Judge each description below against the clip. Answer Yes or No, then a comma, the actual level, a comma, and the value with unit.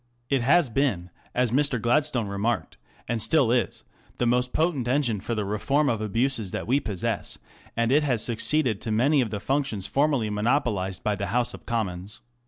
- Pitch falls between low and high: No, low, 120 Hz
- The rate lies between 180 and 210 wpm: Yes, average, 185 wpm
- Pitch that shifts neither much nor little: Yes, average, 4.4 semitones